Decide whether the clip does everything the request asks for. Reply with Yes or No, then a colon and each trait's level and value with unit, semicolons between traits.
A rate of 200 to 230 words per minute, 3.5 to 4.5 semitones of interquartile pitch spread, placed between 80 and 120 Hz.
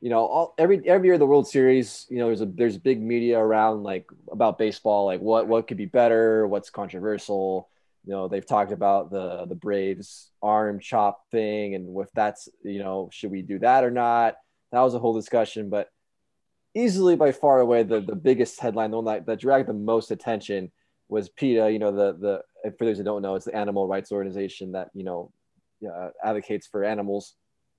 No: fast, 205 wpm; average, 3.0 semitones; low, 110 Hz